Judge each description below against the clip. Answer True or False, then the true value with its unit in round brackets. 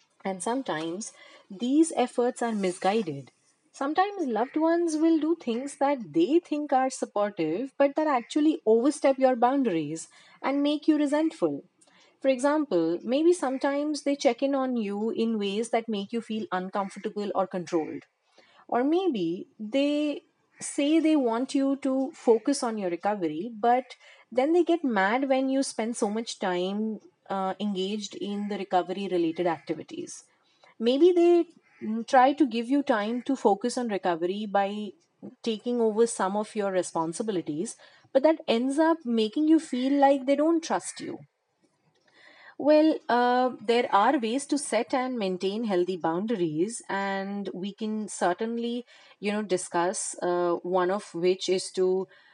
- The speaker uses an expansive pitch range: True (6.3 semitones)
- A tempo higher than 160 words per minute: False (150 wpm)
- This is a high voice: True (235 Hz)